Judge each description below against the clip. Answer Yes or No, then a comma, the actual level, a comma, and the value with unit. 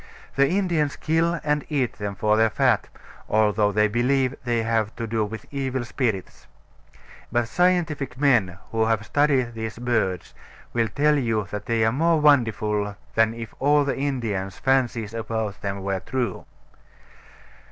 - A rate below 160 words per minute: Yes, average, 150 wpm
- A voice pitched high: No, low, 115 Hz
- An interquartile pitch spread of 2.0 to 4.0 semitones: No, average, 4.5 semitones